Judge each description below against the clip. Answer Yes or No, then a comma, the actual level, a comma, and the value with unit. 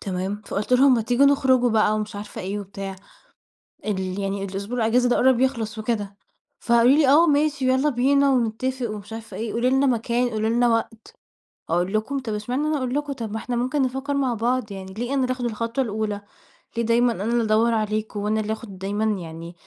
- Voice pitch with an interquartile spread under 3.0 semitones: No, average, 3.4 semitones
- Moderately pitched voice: No, high, 230 Hz